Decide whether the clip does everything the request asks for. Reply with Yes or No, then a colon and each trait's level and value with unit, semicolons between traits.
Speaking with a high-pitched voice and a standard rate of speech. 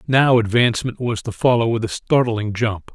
No: low, 115 Hz; average, 185 wpm